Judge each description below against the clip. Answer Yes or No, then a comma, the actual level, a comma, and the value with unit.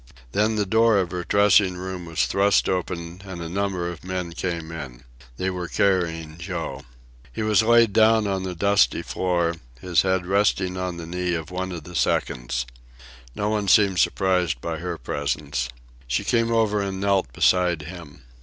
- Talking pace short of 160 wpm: No, average, 175 wpm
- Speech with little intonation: No, average, 3.0 semitones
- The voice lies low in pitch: Yes, very low, 90 Hz